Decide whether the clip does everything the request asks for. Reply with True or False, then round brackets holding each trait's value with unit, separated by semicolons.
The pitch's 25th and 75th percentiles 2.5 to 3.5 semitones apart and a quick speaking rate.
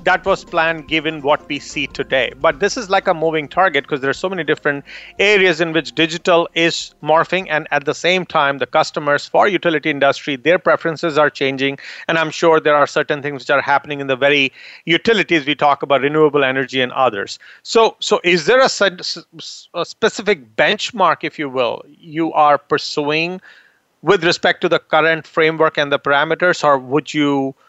False (2.9 semitones; 195 wpm)